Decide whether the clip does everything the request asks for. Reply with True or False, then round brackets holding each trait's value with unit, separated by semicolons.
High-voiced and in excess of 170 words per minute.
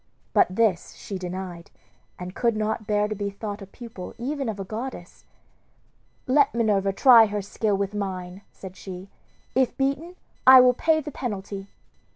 False (210 Hz; 165 wpm)